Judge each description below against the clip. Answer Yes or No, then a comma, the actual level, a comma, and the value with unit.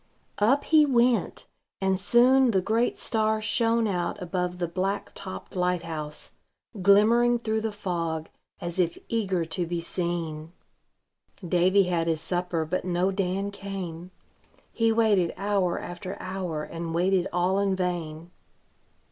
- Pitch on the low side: No, medium, 185 Hz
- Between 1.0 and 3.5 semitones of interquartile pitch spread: Yes, average, 3.2 semitones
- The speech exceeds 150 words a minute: No, average, 140 wpm